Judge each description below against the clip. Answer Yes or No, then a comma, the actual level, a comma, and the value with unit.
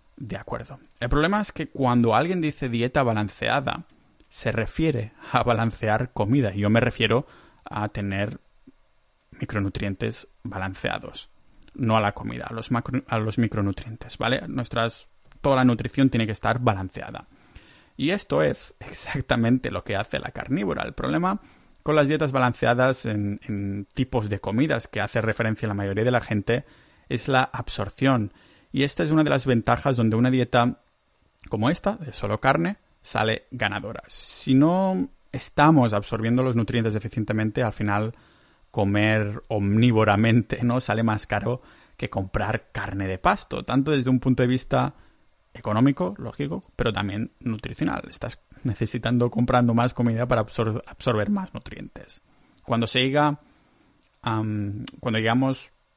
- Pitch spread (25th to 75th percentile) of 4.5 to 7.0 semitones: No, average, 3.2 semitones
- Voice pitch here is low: Yes, low, 120 Hz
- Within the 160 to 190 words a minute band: No, average, 150 wpm